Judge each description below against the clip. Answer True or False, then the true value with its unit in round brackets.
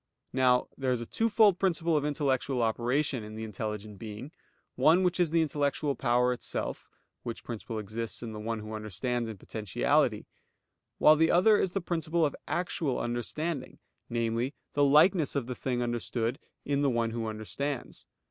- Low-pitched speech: True (125 Hz)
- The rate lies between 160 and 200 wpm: True (165 wpm)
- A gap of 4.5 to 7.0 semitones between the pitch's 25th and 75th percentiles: True (5.1 semitones)